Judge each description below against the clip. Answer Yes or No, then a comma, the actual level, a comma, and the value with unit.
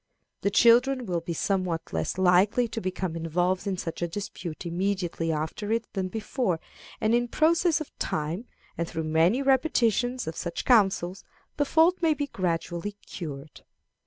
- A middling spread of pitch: No, wide, 6.1 semitones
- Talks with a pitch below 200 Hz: Yes, high, 190 Hz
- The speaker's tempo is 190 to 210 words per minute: No, average, 160 wpm